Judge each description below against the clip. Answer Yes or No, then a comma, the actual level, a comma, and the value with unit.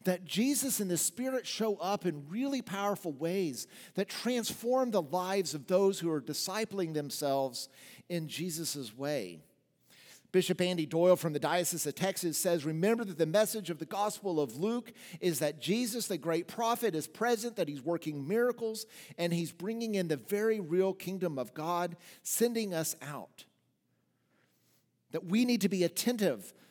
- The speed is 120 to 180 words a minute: Yes, average, 165 wpm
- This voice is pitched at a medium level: Yes, medium, 180 Hz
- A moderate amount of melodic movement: Yes, average, 5.0 semitones